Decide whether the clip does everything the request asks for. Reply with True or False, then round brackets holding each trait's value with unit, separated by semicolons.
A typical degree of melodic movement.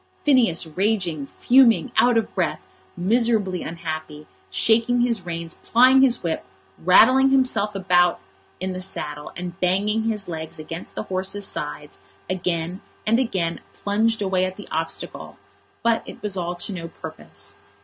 True (5.0 semitones)